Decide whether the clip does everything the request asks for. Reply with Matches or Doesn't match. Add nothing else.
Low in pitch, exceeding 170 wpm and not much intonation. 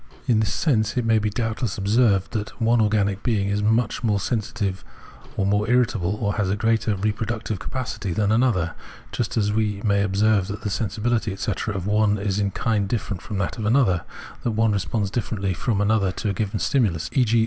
Matches